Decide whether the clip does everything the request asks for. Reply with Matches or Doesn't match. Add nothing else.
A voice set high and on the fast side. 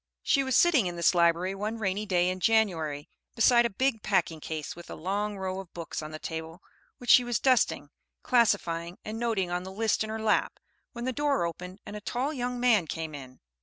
Matches